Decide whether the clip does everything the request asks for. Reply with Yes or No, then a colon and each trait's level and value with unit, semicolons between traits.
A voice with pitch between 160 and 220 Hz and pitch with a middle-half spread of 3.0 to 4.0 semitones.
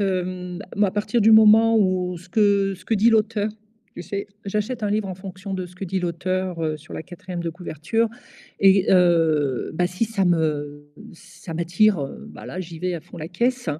Yes: medium, 185 Hz; average, 3.3 semitones